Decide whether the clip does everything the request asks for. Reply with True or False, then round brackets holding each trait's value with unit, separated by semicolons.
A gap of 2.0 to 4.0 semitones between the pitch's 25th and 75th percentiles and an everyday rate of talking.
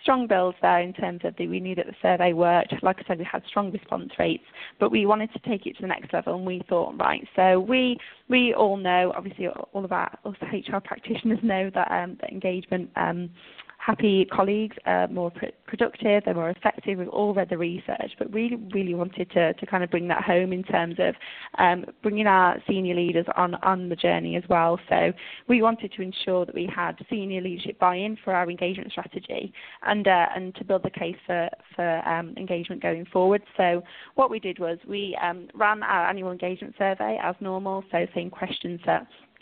False (2.7 semitones; 210 wpm)